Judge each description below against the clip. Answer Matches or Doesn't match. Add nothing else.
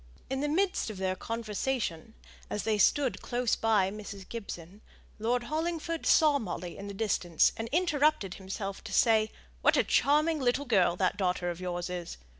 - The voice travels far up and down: Matches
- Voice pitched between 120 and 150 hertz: Doesn't match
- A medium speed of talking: Matches